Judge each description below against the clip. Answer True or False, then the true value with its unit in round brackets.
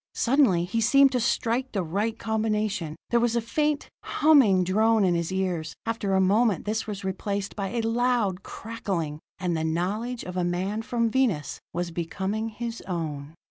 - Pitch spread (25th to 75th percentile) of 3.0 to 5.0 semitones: True (4.3 semitones)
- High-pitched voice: True (210 Hz)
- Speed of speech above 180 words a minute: False (175 wpm)